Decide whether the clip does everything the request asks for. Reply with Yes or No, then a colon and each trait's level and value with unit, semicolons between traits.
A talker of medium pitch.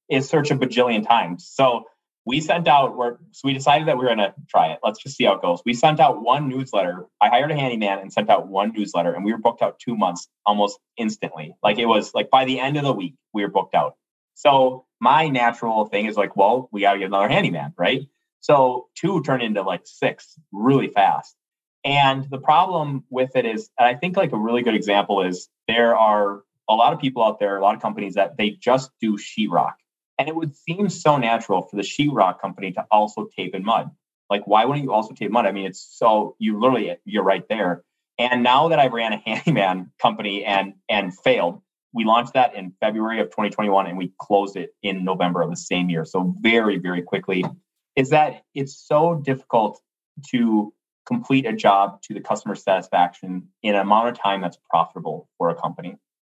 No: low, 115 Hz